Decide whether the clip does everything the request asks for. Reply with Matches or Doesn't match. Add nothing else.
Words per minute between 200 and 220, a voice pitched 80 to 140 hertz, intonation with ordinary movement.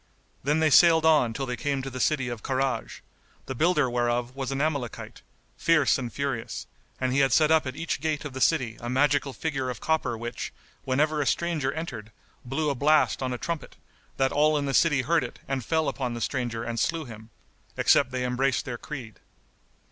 Matches